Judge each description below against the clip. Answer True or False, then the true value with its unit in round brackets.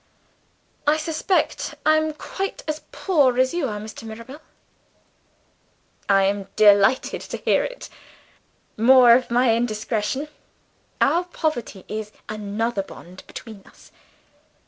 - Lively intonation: True (6.2 semitones)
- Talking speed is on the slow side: True (120 wpm)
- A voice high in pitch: True (240 Hz)